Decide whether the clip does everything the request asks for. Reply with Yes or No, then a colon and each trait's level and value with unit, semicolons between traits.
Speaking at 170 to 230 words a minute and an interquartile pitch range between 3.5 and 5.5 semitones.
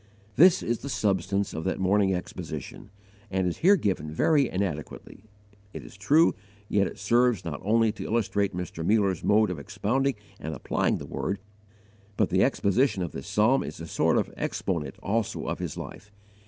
Yes: average, 175 wpm; average, 4.2 semitones